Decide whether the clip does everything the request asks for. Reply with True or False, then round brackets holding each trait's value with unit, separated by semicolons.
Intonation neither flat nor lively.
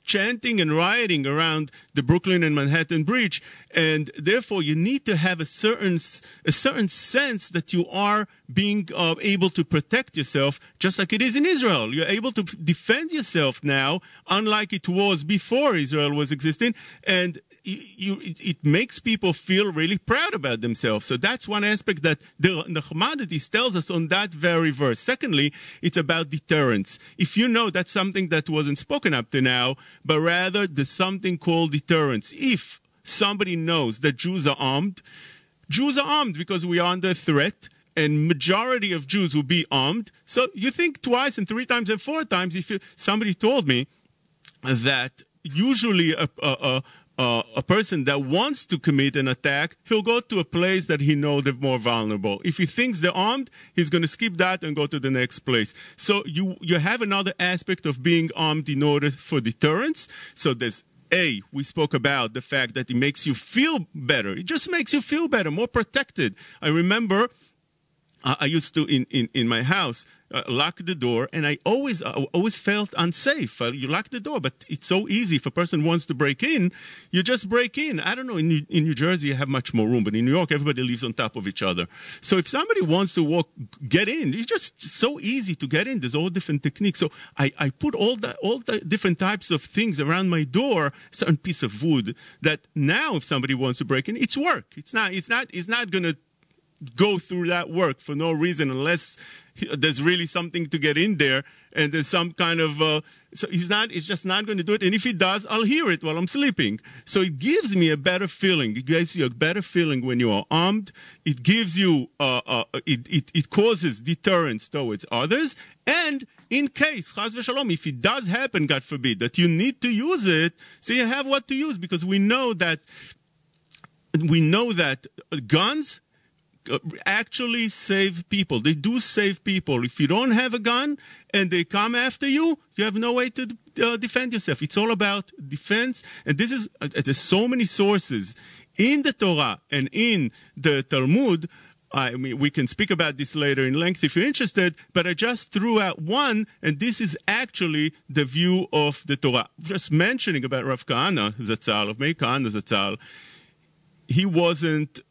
False (5.7 semitones)